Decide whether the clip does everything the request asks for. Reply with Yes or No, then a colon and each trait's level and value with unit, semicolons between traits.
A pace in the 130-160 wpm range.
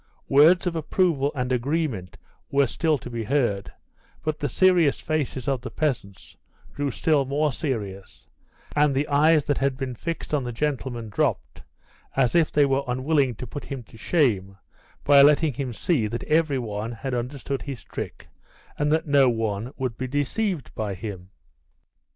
No: average, 170 wpm